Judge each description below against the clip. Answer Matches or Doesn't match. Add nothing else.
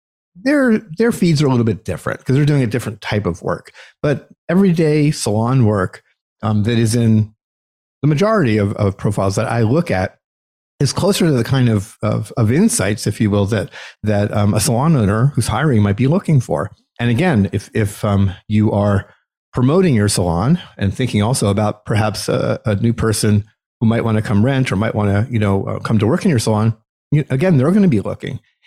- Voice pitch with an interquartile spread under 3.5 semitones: Doesn't match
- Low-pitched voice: Matches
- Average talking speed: Doesn't match